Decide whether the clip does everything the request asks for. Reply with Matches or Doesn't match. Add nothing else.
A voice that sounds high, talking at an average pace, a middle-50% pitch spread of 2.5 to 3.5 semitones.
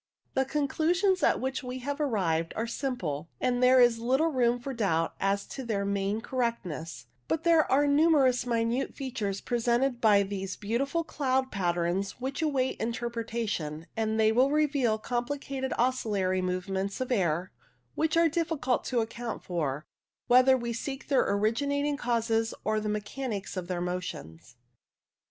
Doesn't match